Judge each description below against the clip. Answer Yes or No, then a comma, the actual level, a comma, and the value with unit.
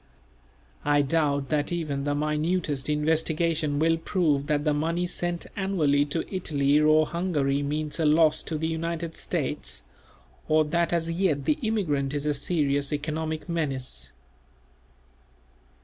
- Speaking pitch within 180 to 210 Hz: No, medium, 155 Hz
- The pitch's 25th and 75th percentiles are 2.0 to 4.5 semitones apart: Yes, narrow, 2.5 semitones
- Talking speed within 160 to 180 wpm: No, slow, 135 wpm